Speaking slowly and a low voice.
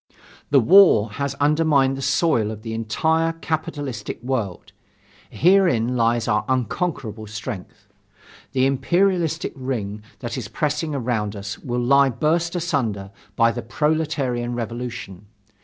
Yes: slow, 125 wpm; low, 130 Hz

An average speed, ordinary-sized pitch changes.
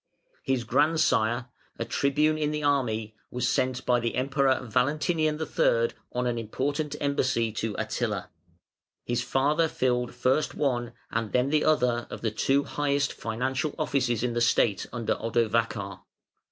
Yes: average, 145 wpm; average, 3.5 semitones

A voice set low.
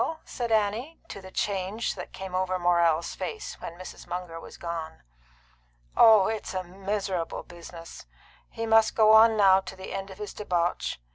No: high, 190 Hz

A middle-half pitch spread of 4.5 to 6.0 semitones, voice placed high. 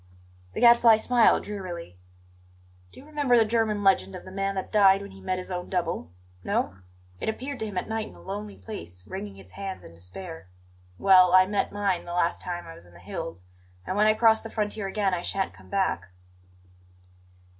No: average, 3.6 semitones; high, 195 Hz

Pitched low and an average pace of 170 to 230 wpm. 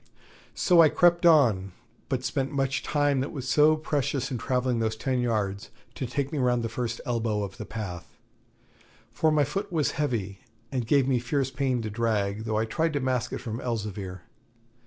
Yes: low, 125 Hz; average, 190 wpm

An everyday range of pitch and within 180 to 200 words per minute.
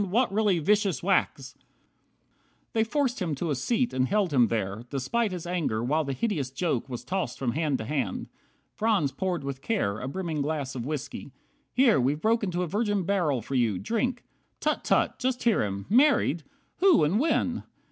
No: wide, 8.0 semitones; average, 190 wpm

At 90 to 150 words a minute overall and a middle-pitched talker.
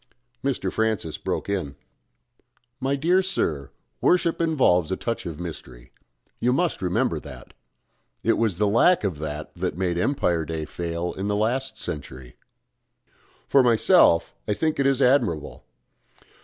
No: average, 140 wpm; low, 100 Hz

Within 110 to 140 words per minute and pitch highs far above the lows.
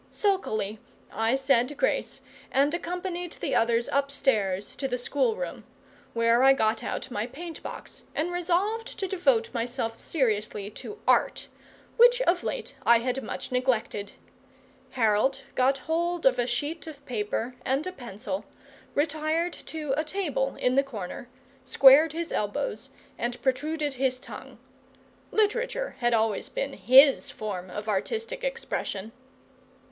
Yes: slow, 135 wpm; wide, 6.3 semitones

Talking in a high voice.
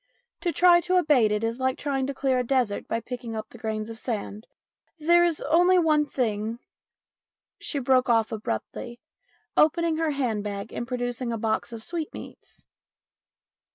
Yes: very high, 250 Hz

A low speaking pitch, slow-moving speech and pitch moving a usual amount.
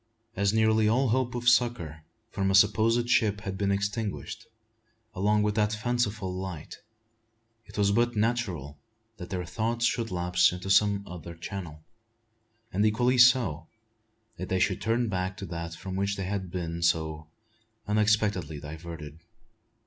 No: low, 100 Hz; average, 150 wpm; average, 3.9 semitones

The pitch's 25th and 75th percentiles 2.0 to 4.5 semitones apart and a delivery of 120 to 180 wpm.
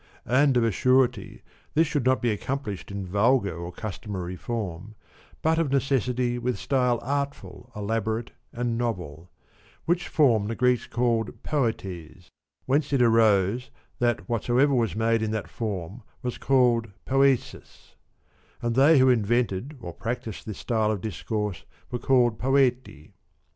Yes: average, 3.6 semitones; average, 145 wpm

